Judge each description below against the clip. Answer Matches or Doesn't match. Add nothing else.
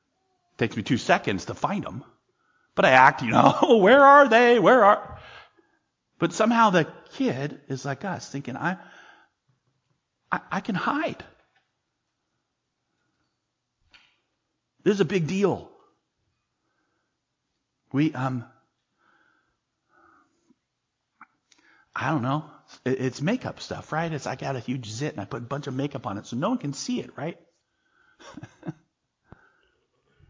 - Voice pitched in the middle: Matches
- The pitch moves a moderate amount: Doesn't match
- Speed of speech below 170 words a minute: Matches